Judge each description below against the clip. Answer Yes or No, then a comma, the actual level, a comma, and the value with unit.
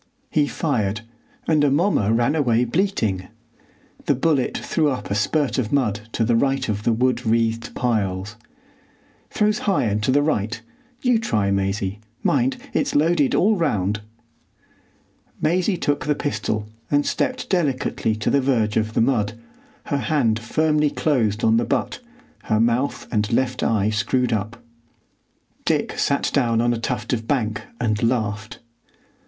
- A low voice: Yes, low, 120 Hz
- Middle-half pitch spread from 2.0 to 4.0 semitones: No, average, 5.1 semitones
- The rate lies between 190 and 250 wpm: No, average, 150 wpm